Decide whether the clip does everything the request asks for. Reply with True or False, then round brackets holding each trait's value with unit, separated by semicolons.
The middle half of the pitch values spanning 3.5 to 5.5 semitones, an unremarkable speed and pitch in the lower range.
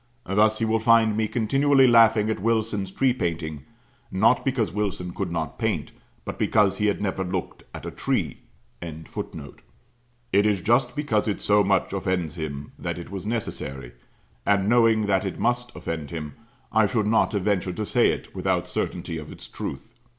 True (3.9 semitones; 175 wpm; 105 Hz)